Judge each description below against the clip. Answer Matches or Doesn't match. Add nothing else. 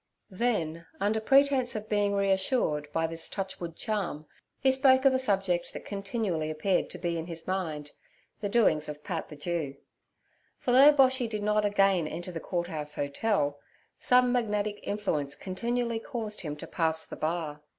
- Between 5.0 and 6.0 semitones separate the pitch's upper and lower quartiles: Matches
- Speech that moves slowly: Doesn't match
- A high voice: Matches